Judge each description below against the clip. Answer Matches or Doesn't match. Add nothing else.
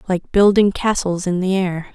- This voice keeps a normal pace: Matches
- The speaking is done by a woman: Matches